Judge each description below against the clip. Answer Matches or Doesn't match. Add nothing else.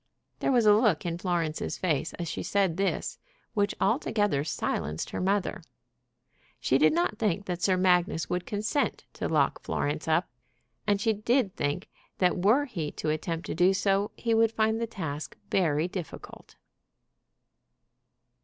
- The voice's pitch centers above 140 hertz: Matches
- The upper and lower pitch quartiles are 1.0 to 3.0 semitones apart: Doesn't match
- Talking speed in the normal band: Matches